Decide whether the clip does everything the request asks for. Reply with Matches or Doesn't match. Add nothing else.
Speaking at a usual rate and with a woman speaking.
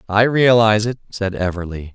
Doesn't match